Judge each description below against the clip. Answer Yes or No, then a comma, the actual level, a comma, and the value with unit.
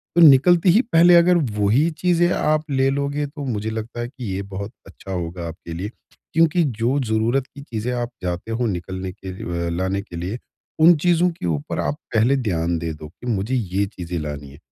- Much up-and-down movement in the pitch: Yes, wide, 7.9 semitones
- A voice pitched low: Yes, low, 110 Hz